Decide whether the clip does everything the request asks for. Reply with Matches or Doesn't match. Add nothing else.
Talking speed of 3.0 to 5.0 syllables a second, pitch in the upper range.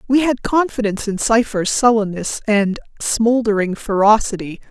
Matches